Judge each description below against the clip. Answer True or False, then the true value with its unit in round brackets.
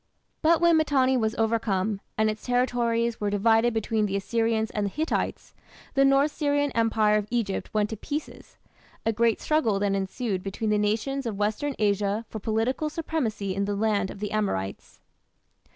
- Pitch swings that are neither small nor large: True (3.5 semitones)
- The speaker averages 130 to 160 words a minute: False (170 wpm)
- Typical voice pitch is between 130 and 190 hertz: False (220 Hz)